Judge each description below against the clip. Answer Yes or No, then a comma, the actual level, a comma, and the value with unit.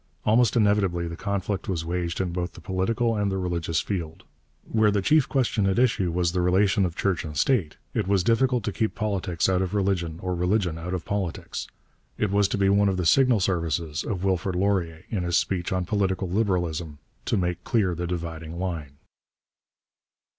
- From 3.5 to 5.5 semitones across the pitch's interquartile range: No, average, 2.9 semitones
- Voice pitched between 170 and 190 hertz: No, very low, 95 Hz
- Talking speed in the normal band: Yes, average, 190 wpm